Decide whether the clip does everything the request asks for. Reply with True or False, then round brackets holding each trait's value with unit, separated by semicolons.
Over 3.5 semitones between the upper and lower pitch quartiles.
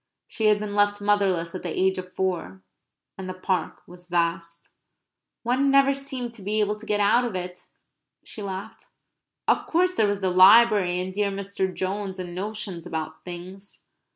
False (2.6 semitones)